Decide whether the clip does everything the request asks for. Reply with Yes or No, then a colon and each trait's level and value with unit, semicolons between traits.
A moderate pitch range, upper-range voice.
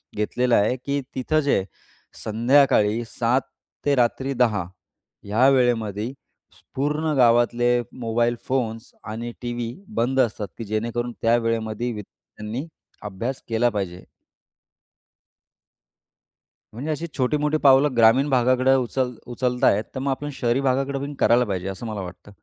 No: average, 3.0 semitones; low, 120 Hz